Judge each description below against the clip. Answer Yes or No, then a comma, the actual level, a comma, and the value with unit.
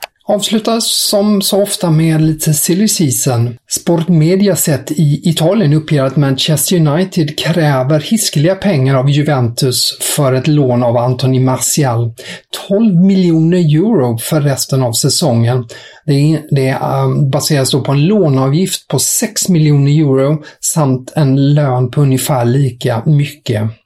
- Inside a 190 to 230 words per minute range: No, slow, 135 wpm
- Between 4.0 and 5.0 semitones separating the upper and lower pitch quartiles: Yes, average, 4.4 semitones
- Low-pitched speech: No, medium, 150 Hz